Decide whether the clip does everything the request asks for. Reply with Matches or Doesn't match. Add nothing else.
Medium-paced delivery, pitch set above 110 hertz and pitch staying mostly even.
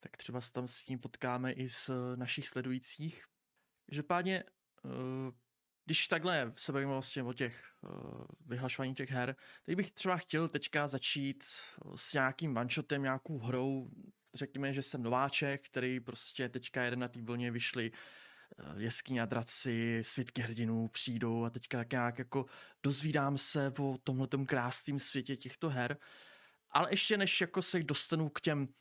Doesn't match